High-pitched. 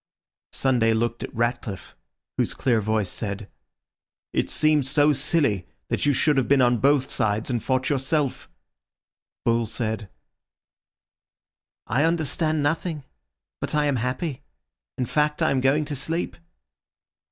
No: low, 130 Hz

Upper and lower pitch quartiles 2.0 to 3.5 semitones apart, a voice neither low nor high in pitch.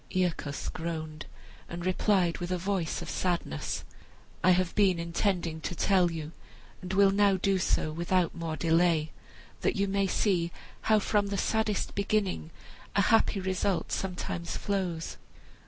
Yes: average, 2.8 semitones; medium, 180 Hz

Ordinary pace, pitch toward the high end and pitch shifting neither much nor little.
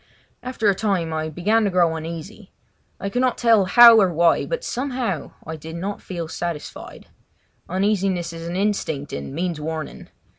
No: average, 165 wpm; medium, 180 Hz; average, 4.7 semitones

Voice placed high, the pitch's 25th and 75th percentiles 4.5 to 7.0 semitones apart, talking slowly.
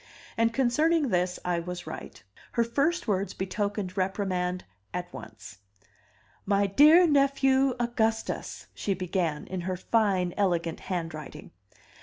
Yes: high, 195 Hz; average, 5.1 semitones; slow, 120 wpm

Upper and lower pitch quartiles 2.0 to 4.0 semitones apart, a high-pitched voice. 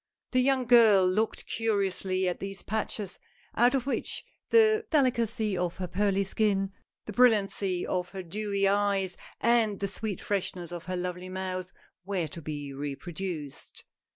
Yes: average, 3.2 semitones; high, 195 Hz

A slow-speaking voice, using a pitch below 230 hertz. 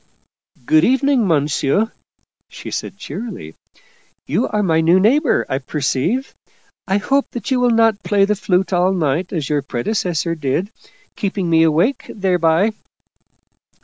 No: average, 145 wpm; medium, 185 Hz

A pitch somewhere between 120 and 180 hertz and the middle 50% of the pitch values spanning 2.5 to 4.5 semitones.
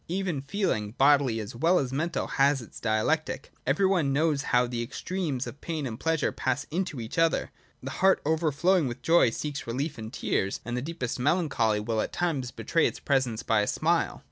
No: medium, 140 Hz; wide, 5.4 semitones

